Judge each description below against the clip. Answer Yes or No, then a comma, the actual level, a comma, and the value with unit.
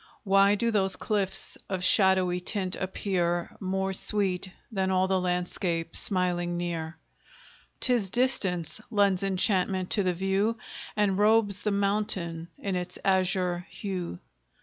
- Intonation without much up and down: Yes, narrow, 2.0 semitones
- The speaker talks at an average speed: No, slow, 125 wpm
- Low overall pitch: No, high, 190 Hz